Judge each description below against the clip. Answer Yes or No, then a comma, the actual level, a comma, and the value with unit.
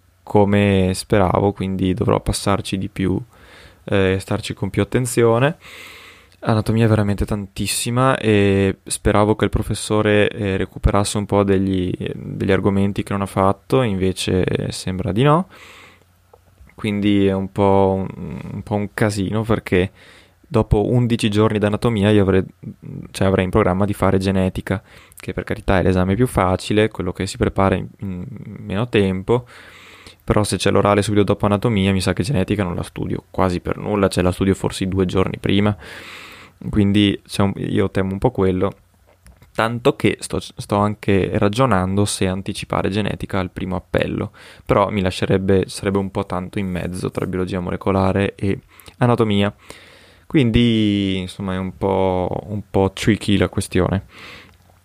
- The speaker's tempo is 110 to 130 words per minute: No, average, 155 wpm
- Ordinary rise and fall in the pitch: No, narrow, 2.0 semitones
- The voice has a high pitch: No, low, 100 Hz